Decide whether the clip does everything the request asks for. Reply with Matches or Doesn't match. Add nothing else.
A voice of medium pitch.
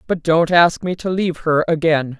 Matches